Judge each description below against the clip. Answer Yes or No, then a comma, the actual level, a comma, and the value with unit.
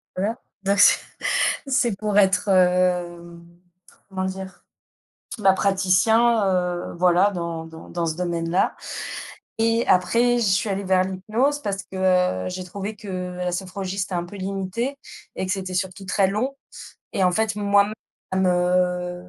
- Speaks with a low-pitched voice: No, high, 190 Hz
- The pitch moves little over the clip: Yes, narrow, 2.1 semitones